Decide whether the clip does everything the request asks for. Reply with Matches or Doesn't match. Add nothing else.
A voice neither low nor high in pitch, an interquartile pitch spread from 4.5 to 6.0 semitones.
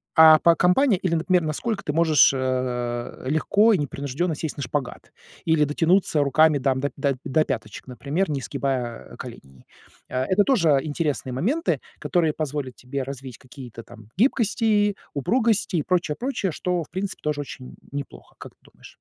Matches